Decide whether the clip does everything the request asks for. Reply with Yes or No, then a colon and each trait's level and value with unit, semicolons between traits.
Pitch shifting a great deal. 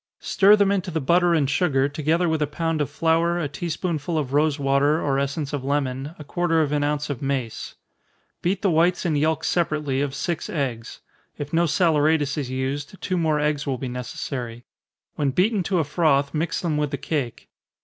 No: average, 3.2 semitones